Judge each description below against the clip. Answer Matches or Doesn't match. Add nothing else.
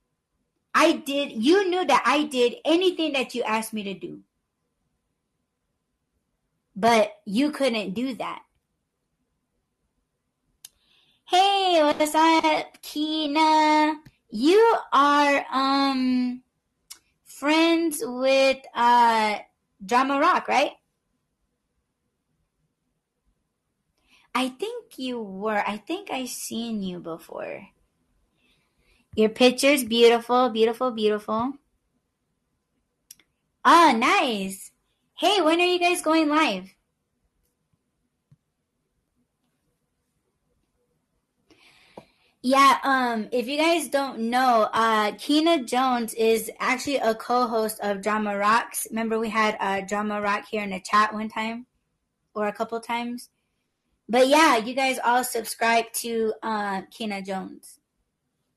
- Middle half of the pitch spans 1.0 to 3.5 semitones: Doesn't match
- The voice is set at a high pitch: Matches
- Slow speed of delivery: Matches